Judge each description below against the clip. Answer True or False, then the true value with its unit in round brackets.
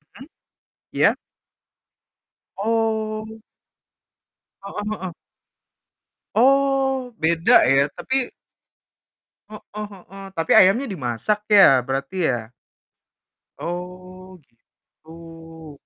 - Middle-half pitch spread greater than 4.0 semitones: True (5.0 semitones)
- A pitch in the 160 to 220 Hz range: True (190 Hz)